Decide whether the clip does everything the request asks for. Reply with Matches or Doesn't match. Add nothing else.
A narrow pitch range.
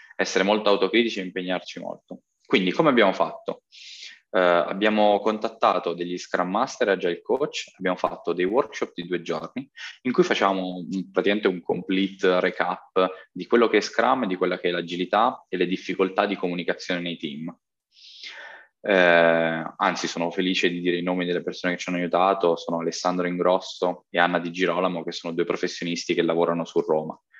Matches